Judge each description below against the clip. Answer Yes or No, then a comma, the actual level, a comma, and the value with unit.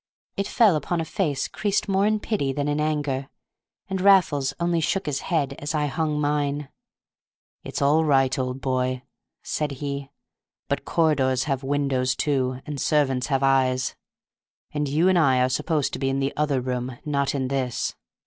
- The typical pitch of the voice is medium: Yes, medium, 145 Hz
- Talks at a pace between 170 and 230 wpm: Yes, average, 175 wpm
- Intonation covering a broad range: No, narrow, 2.6 semitones